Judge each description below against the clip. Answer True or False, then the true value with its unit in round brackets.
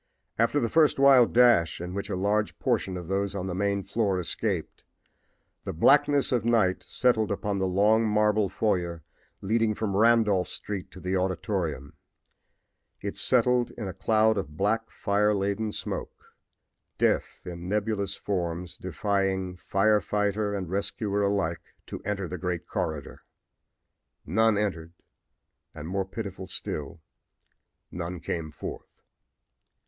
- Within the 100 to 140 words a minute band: True (135 wpm)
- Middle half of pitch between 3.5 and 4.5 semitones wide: False (3.0 semitones)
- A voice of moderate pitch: False (100 Hz)